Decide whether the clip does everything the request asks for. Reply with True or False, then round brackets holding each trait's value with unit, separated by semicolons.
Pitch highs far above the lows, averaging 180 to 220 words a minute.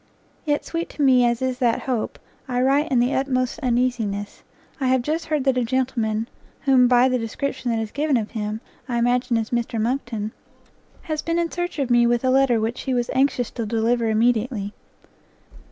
False (2.7 semitones; 195 wpm)